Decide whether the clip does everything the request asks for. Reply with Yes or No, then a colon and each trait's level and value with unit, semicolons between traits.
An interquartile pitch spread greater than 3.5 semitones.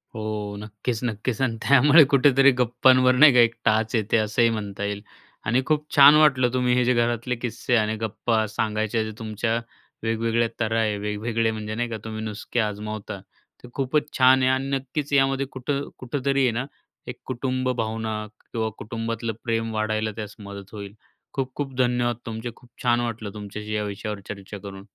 No: average, 3.0 semitones